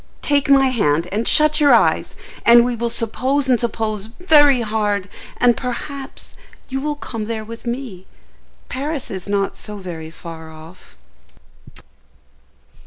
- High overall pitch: Yes, high, 235 Hz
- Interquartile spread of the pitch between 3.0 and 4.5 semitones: No, average, 5.0 semitones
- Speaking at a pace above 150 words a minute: No, average, 140 wpm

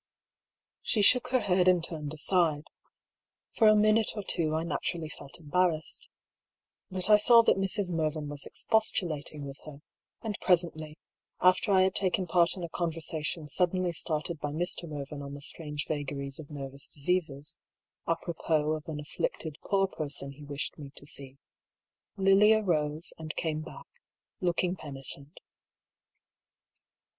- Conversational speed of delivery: Yes, average, 145 wpm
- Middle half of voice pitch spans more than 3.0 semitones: Yes, average, 3.8 semitones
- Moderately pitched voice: Yes, medium, 160 Hz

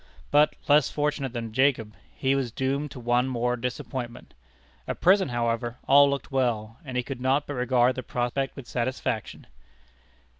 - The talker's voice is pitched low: Yes, low, 130 Hz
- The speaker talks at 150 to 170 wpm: Yes, average, 160 wpm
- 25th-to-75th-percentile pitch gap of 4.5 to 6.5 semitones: No, narrow, 2.4 semitones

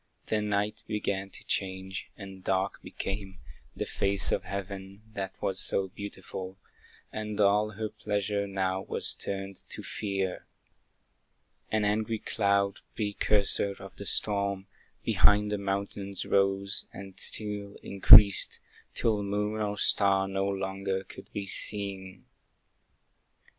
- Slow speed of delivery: Yes, slow, 120 wpm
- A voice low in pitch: Yes, low, 100 Hz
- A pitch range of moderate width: No, narrow, 1.1 semitones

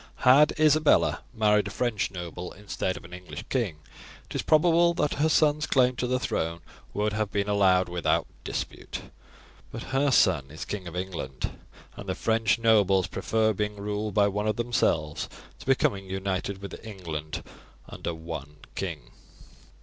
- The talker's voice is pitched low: Yes, low, 105 Hz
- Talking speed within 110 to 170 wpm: Yes, average, 160 wpm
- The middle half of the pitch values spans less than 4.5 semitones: No, average, 4.8 semitones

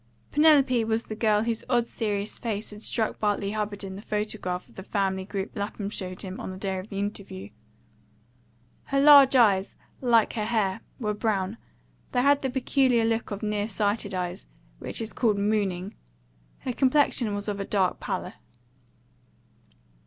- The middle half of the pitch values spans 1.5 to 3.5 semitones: Yes, average, 2.8 semitones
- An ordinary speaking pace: Yes, average, 165 wpm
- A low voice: No, high, 210 Hz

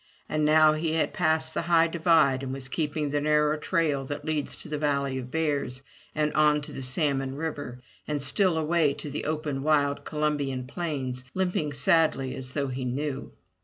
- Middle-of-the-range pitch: Yes, medium, 150 Hz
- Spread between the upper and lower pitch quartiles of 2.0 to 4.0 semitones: Yes, narrow, 2.6 semitones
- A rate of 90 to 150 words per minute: No, average, 180 wpm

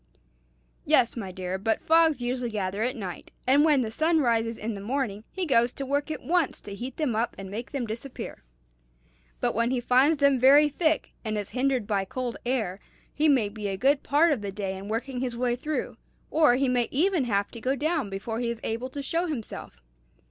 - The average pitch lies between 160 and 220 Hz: No, high, 245 Hz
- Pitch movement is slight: No, average, 4.6 semitones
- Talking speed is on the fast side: Yes, fast, 215 wpm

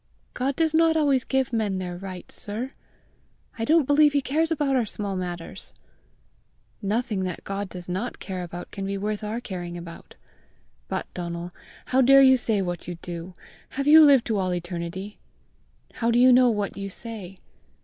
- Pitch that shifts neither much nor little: No, wide, 6.3 semitones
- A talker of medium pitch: No, high, 210 Hz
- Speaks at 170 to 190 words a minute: Yes, average, 180 wpm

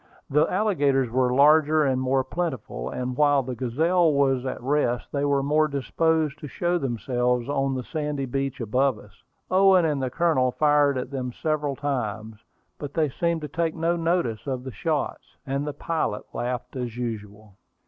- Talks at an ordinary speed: Yes, average, 175 wpm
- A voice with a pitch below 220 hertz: Yes, medium, 140 Hz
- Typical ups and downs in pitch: Yes, average, 3.5 semitones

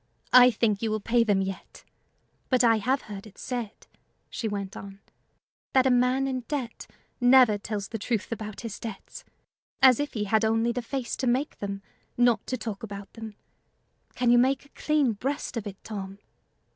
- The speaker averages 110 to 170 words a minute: No, average, 185 wpm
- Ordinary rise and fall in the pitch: Yes, average, 3.4 semitones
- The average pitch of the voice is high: Yes, high, 230 Hz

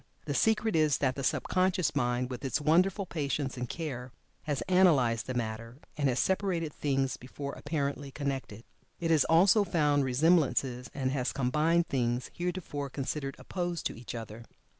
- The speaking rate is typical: Yes, average, 160 wpm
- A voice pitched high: No, medium, 140 Hz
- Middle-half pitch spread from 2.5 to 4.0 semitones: No, average, 4.6 semitones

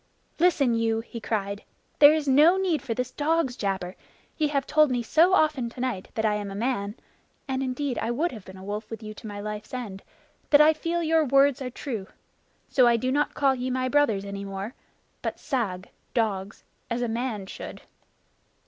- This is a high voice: Yes, high, 245 Hz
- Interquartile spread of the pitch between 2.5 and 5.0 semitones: No, wide, 5.5 semitones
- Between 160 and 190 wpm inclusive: No, average, 200 wpm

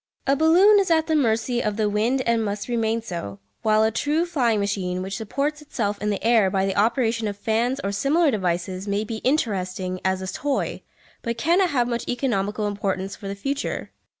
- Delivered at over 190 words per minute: Yes, average, 200 wpm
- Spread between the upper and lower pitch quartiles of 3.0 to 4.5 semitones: No, average, 4.9 semitones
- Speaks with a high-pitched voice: Yes, high, 220 Hz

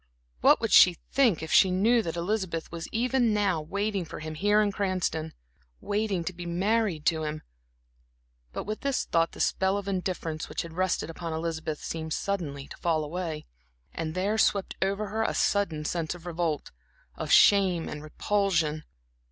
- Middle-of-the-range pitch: Yes, medium, 175 Hz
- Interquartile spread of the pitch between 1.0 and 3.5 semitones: No, average, 4.0 semitones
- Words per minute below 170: No, average, 175 wpm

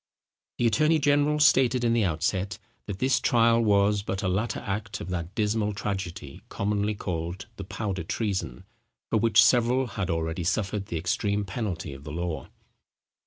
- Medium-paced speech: Yes, average, 165 wpm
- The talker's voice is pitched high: No, low, 100 Hz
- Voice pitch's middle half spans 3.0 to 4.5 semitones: Yes, average, 3.9 semitones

